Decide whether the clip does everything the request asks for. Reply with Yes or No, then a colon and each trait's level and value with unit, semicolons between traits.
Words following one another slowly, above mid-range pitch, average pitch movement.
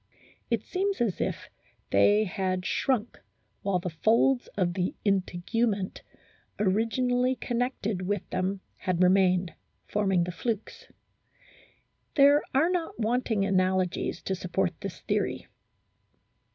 Yes: slow, 110 wpm; high, 200 Hz; average, 4.5 semitones